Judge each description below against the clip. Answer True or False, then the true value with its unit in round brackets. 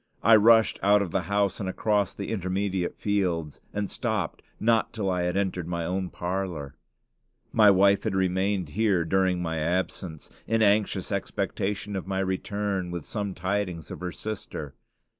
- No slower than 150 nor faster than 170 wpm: True (160 wpm)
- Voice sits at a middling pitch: False (95 Hz)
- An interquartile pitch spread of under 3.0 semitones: True (2.5 semitones)